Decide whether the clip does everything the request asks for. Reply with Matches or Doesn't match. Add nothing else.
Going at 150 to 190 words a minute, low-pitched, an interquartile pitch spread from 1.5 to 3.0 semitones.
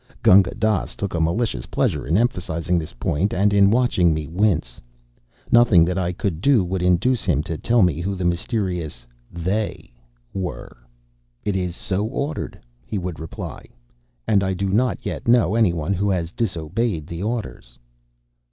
Doesn't match